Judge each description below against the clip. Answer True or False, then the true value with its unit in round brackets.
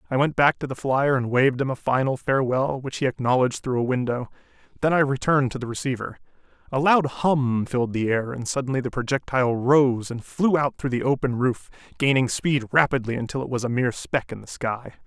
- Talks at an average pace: False (215 wpm)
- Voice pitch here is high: False (130 Hz)